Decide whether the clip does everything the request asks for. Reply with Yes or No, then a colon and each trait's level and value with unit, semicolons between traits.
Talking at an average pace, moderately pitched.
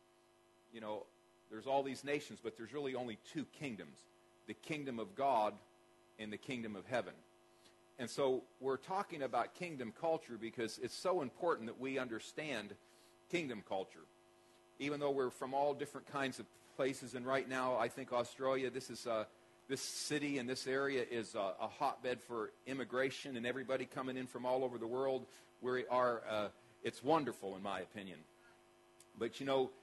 No: average, 170 wpm; low, 130 Hz